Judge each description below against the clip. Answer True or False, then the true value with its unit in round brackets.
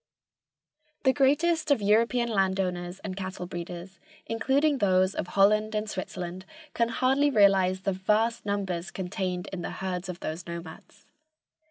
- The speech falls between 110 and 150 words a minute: True (140 wpm)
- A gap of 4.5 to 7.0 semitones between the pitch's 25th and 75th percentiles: False (3.8 semitones)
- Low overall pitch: False (195 Hz)